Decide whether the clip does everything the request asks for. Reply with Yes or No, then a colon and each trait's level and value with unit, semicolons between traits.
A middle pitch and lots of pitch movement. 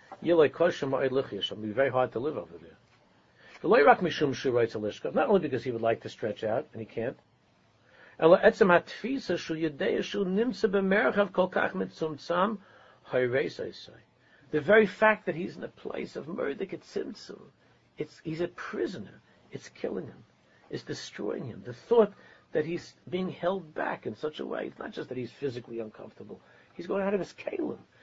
Yes: medium, 170 Hz; wide, 7.3 semitones